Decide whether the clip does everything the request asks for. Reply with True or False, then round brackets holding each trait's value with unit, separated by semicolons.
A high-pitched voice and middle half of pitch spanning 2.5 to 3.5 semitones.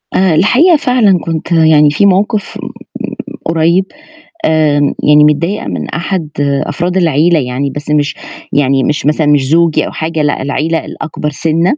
False (160 Hz; 3.0 semitones)